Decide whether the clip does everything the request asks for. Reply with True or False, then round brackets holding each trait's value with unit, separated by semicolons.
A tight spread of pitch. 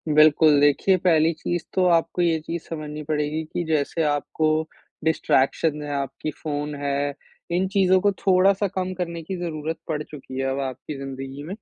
False (3.1 semitones)